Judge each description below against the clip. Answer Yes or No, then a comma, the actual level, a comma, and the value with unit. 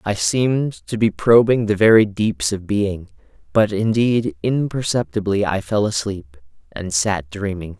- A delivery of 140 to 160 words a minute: Yes, average, 145 wpm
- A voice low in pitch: Yes, low, 100 Hz